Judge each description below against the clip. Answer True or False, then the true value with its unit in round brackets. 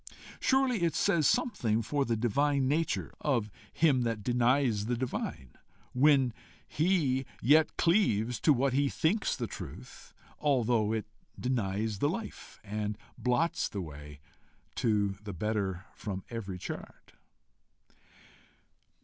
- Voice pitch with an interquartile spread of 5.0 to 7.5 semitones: True (5.6 semitones)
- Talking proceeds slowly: True (125 wpm)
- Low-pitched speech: True (120 Hz)